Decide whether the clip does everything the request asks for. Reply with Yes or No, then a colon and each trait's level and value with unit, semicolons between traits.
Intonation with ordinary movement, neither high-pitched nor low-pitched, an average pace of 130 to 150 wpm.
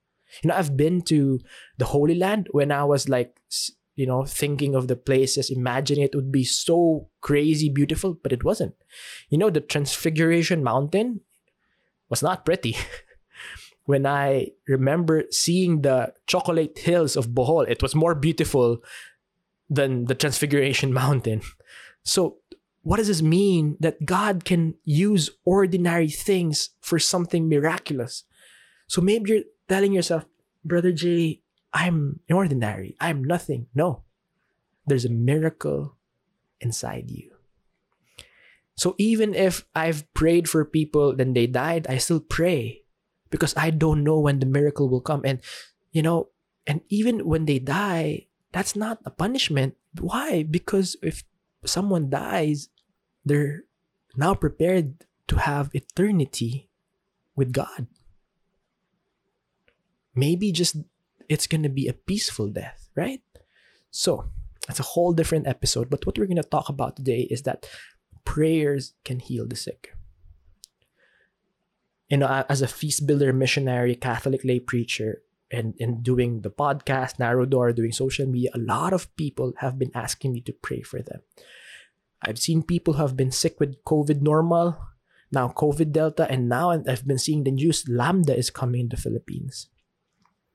Yes: average, 4.5 semitones; medium, 150 Hz; average, 145 wpm